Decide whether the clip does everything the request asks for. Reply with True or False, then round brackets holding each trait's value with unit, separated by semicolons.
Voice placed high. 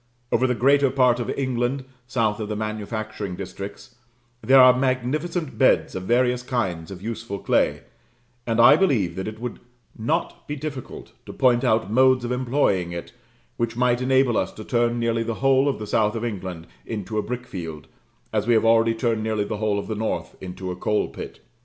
False (115 Hz)